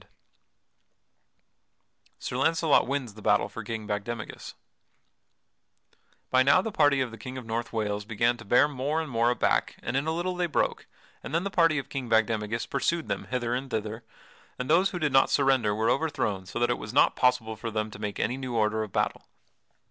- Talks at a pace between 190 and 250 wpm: Yes, average, 200 wpm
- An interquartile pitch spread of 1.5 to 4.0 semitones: No, average, 4.4 semitones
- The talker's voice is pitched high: No, low, 120 Hz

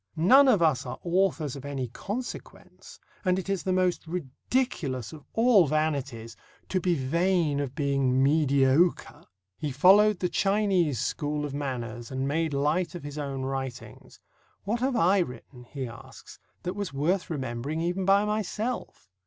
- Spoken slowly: No, average, 155 wpm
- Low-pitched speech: No, medium, 155 Hz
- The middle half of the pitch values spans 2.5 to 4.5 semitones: No, wide, 5.6 semitones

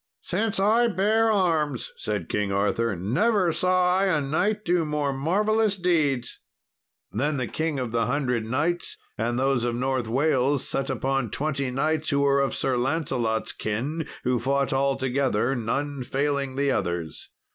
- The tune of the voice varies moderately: Yes, average, 5.0 semitones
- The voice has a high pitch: No, medium, 140 Hz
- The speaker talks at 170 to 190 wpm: No, average, 155 wpm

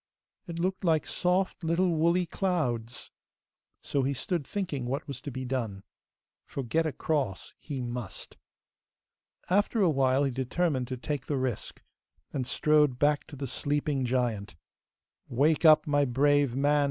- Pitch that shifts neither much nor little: Yes, average, 3.9 semitones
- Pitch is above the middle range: No, medium, 145 Hz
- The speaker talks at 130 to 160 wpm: Yes, average, 150 wpm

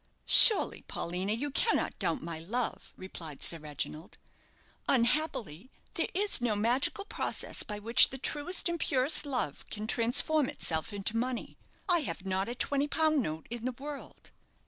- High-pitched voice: Yes, high, 240 Hz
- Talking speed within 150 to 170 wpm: Yes, average, 155 wpm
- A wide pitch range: Yes, wide, 7.1 semitones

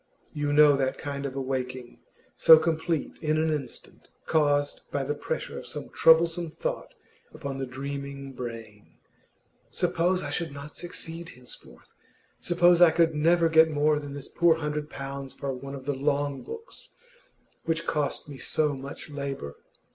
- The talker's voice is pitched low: No, medium, 145 Hz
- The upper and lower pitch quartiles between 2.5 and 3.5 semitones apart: Yes, average, 2.8 semitones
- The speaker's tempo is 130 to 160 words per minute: Yes, average, 155 wpm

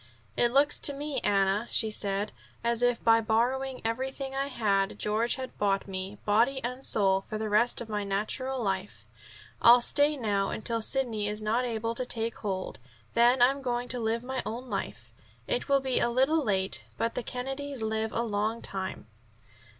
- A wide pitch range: No, average, 3.6 semitones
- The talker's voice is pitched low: No, high, 230 Hz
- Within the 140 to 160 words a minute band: No, average, 180 wpm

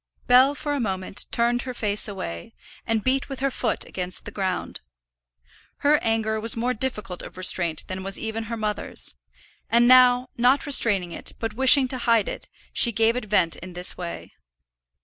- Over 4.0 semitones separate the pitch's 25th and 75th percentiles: Yes, average, 4.4 semitones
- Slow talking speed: No, average, 180 wpm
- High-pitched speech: Yes, high, 225 Hz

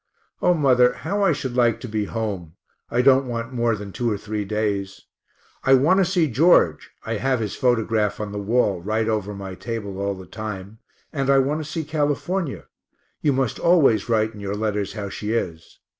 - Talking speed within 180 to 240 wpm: Yes, average, 200 wpm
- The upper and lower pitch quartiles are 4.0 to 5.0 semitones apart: Yes, average, 4.6 semitones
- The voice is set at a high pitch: No, low, 115 Hz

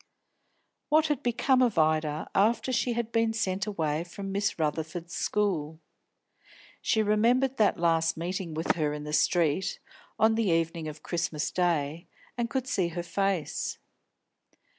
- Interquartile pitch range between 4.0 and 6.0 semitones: Yes, wide, 5.6 semitones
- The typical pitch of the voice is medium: Yes, medium, 180 Hz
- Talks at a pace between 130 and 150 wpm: Yes, average, 145 wpm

